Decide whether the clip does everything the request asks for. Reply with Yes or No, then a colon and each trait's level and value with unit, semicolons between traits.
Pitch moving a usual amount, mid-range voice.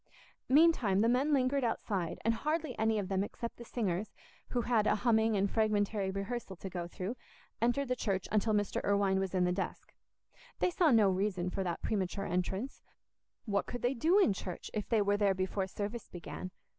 No: average, 3.8 semitones; high, 210 Hz